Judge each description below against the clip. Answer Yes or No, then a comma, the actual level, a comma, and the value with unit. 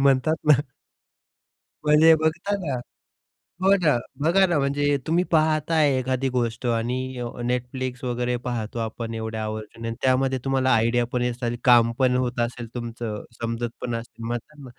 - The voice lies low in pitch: Yes, low, 125 Hz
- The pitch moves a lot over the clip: No, average, 3.4 semitones